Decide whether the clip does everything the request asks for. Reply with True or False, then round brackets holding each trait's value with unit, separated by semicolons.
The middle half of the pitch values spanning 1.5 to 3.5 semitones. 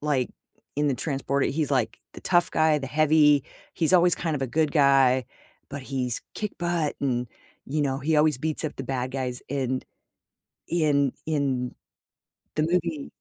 True (2.9 semitones)